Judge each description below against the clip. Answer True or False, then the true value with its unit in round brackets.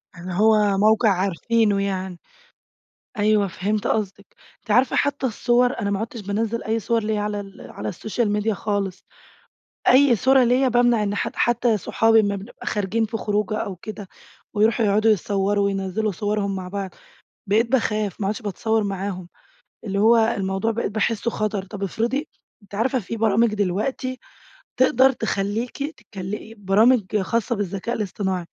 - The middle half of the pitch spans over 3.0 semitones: False (2.4 semitones)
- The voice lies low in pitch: False (210 Hz)